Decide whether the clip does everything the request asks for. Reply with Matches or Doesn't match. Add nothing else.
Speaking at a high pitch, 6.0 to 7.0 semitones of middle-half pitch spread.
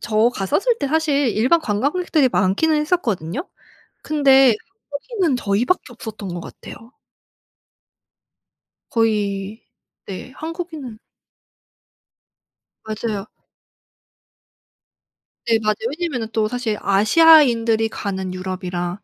Matches